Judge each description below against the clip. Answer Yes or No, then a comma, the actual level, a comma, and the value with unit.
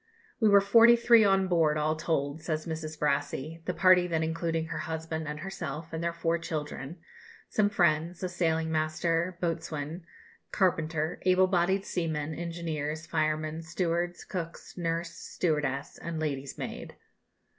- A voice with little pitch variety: Yes, narrow, 2.1 semitones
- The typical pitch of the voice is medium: Yes, medium, 165 Hz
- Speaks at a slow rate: No, average, 145 wpm